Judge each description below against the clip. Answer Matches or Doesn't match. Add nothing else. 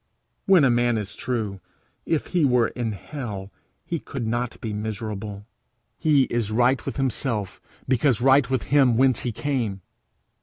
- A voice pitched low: Matches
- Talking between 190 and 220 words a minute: Doesn't match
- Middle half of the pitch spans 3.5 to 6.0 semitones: Matches